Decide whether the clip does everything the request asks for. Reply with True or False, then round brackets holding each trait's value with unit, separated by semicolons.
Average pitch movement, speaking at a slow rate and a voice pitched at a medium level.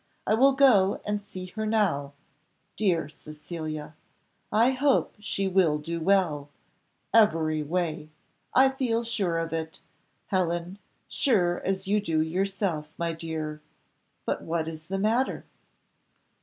True (4.6 semitones; 130 wpm; 180 Hz)